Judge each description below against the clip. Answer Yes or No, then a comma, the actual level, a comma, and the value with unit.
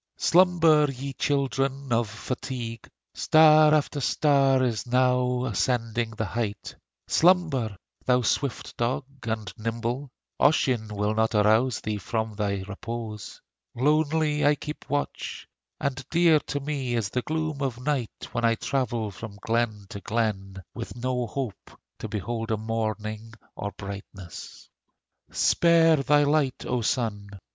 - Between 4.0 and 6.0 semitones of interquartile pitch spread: Yes, average, 4.3 semitones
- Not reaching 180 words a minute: Yes, slow, 135 wpm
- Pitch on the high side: No, low, 120 Hz